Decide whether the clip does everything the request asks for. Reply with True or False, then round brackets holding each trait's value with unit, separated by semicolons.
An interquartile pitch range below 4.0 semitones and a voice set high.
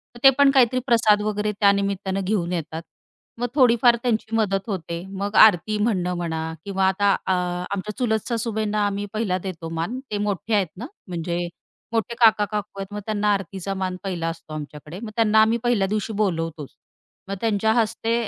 True (3.1 semitones; 205 Hz)